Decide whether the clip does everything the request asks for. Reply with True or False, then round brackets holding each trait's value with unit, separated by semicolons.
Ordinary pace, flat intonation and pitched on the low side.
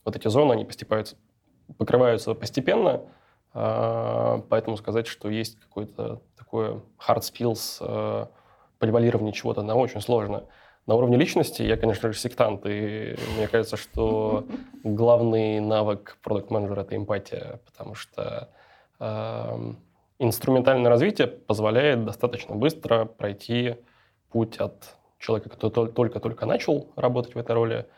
True (120 wpm; 1.9 semitones; 115 Hz)